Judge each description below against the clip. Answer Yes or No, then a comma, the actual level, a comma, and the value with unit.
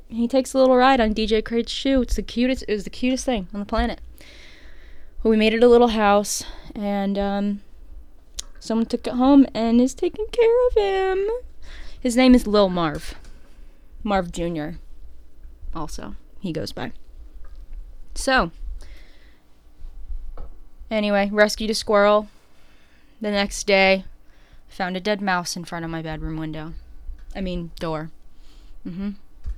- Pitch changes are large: Yes, wide, 7.7 semitones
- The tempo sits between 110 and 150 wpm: Yes, average, 145 wpm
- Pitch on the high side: Yes, high, 200 Hz